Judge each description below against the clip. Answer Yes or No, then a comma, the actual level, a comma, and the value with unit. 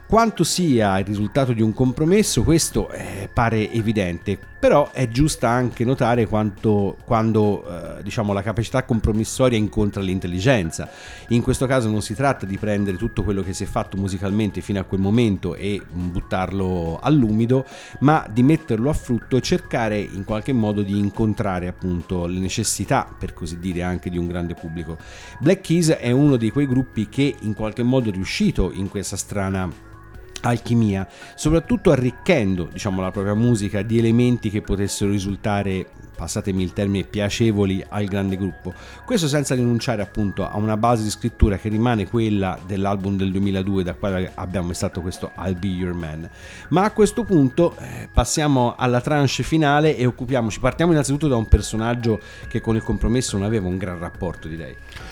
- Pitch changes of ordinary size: Yes, average, 4.3 semitones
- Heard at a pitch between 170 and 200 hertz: No, low, 105 Hz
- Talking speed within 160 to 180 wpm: Yes, fast, 170 wpm